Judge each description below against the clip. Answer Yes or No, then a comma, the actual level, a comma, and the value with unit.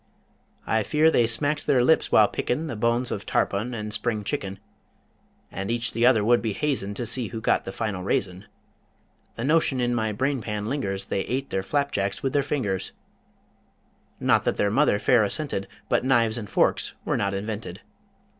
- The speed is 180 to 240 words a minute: Yes, average, 185 wpm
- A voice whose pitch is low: Yes, low, 115 Hz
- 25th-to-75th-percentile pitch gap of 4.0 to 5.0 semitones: Yes, average, 4.3 semitones